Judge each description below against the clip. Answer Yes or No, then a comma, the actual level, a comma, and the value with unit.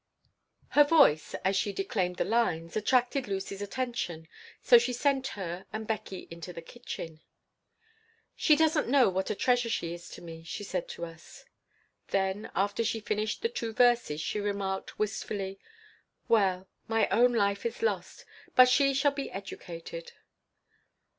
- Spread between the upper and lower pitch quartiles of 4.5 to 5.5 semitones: Yes, average, 4.9 semitones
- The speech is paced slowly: No, average, 155 wpm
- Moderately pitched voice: No, high, 205 Hz